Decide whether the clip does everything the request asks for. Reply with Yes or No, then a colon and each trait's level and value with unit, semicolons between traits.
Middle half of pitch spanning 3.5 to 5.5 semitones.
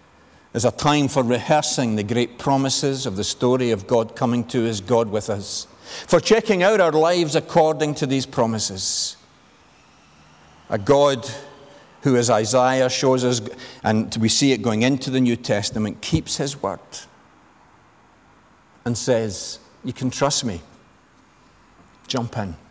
Yes: average, 3.8 semitones